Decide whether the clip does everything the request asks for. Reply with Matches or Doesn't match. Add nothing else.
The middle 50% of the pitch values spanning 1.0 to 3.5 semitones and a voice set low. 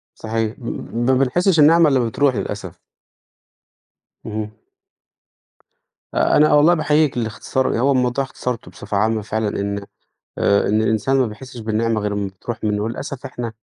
Doesn't match